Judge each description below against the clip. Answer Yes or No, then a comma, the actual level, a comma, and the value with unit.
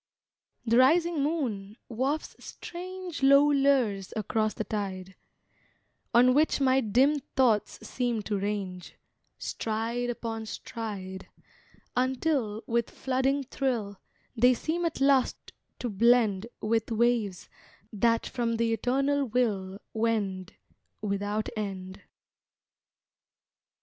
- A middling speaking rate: No, slow, 105 wpm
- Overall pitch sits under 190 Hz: No, high, 230 Hz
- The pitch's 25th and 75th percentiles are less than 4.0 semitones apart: No, average, 4.3 semitones